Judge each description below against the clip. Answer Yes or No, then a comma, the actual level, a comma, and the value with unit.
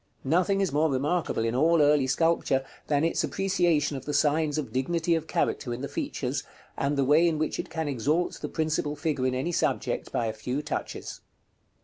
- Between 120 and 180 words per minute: No, average, 200 wpm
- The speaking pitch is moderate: Yes, medium, 150 Hz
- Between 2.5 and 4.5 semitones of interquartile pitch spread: Yes, average, 3.4 semitones